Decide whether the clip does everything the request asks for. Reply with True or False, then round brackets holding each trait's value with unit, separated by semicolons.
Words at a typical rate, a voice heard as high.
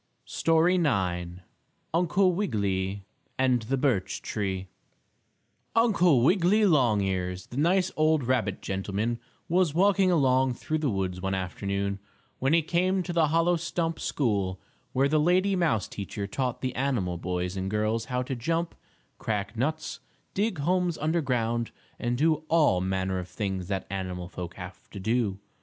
False (150 wpm; 125 Hz)